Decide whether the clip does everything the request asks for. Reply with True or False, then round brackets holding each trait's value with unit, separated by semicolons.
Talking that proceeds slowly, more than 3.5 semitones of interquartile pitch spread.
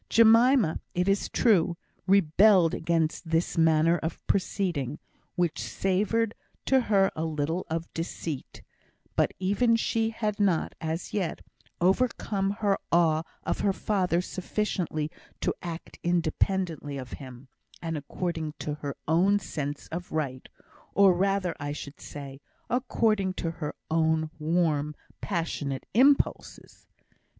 True (125 wpm; 4.0 semitones)